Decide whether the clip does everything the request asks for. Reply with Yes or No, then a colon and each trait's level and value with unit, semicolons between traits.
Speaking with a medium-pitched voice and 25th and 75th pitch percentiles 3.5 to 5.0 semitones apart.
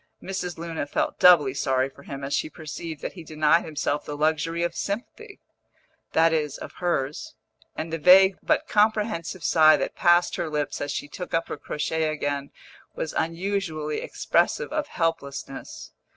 No: medium, 160 Hz; average, 3.1 semitones